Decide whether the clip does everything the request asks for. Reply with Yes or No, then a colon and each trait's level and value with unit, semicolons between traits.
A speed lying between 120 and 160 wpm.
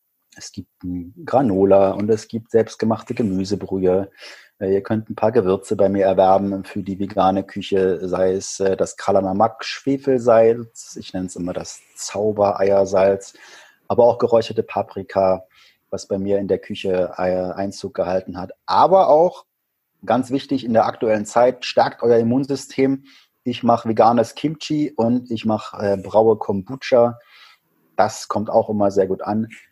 Yes: average, 140 wpm